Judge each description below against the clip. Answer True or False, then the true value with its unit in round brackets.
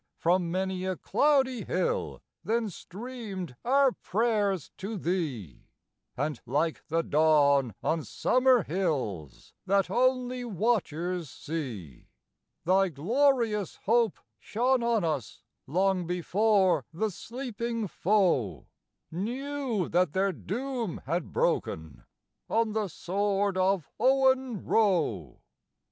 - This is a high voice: True (195 Hz)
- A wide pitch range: True (6.2 semitones)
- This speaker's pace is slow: True (105 wpm)